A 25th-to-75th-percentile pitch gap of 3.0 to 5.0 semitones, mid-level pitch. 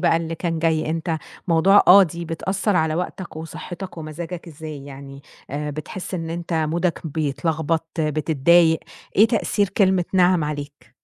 No: narrow, 2.4 semitones; medium, 165 Hz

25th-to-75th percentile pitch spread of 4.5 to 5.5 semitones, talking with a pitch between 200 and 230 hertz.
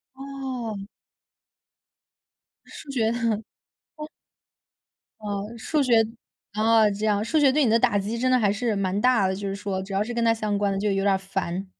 No: average, 3.2 semitones; high, 215 Hz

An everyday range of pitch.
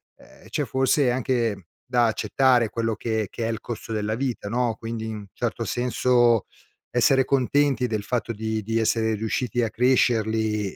No: narrow, 2.2 semitones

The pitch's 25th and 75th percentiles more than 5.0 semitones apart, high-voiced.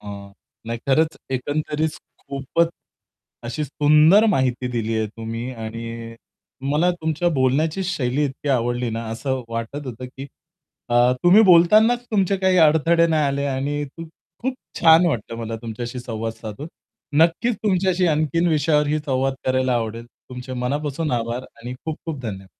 No: wide, 5.4 semitones; medium, 140 Hz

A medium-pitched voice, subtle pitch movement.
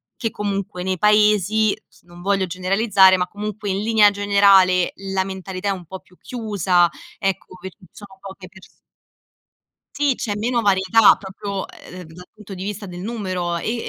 No: high, 195 Hz; narrow, 2.2 semitones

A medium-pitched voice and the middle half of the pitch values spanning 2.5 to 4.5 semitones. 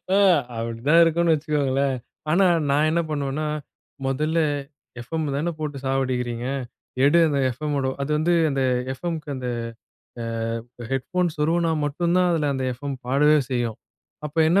Yes: medium, 145 Hz; average, 3.4 semitones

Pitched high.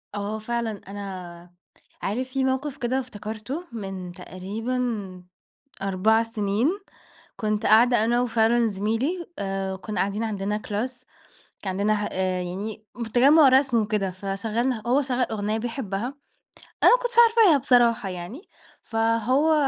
Yes: high, 220 Hz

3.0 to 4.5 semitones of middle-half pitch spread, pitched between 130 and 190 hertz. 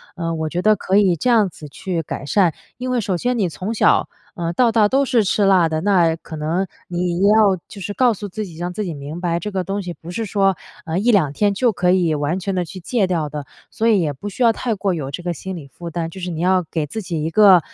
Yes: average, 3.8 semitones; medium, 185 Hz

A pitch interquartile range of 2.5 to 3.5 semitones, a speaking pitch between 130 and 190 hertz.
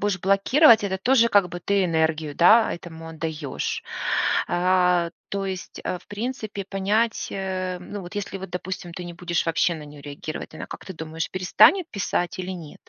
Yes: average, 3.0 semitones; medium, 185 Hz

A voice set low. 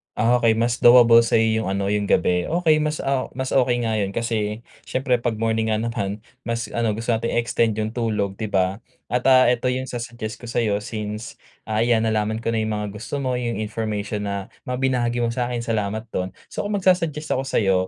Yes: low, 115 Hz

